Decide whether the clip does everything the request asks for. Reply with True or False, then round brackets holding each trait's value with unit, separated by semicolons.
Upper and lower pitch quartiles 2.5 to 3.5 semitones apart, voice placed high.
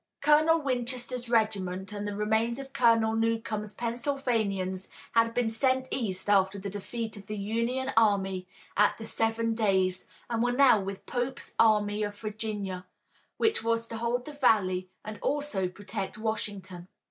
True (3.1 semitones; 220 Hz)